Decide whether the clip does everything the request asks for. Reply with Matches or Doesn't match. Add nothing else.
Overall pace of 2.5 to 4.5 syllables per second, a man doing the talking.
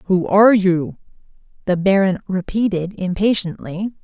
Doesn't match